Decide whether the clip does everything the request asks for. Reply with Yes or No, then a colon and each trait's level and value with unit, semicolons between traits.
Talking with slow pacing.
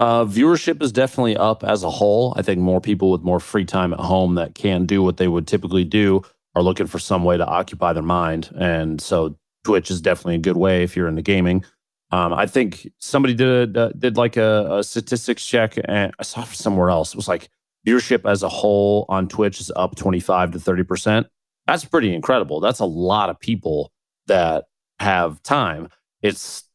No: fast, 205 wpm